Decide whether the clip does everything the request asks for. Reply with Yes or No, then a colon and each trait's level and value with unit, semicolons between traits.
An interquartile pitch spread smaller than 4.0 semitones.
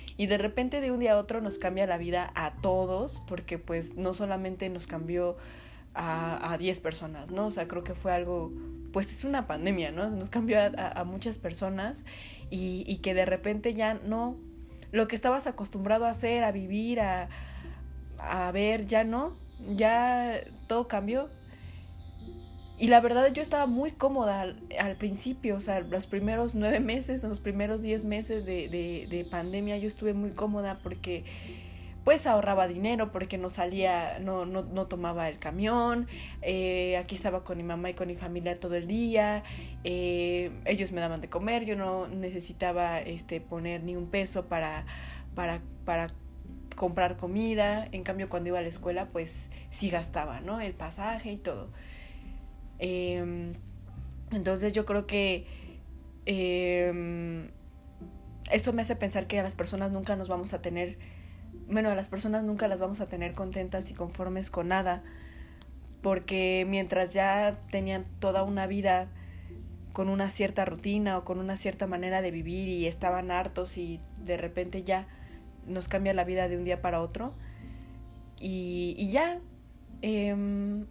Yes: average, 3.6 semitones